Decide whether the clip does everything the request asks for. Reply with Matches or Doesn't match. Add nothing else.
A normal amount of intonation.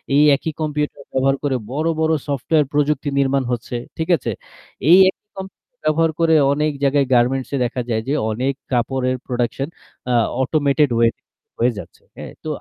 Matches